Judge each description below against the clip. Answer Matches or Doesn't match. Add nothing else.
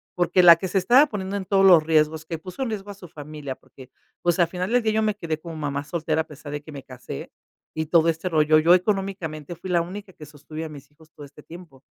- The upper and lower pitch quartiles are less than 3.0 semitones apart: Doesn't match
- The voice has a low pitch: Doesn't match